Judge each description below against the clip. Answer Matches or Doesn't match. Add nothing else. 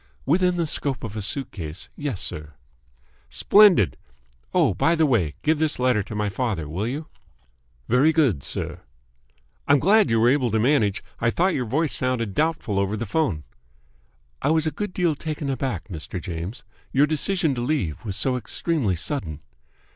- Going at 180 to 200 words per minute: Doesn't match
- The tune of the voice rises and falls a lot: Matches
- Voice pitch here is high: Doesn't match